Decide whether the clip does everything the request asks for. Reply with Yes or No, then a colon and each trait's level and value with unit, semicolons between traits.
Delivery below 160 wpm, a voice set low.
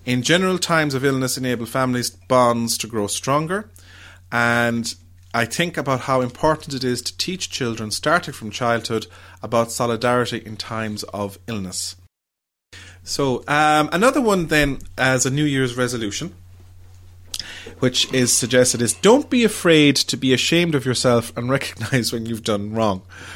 Yes: average, 150 wpm; low, 120 Hz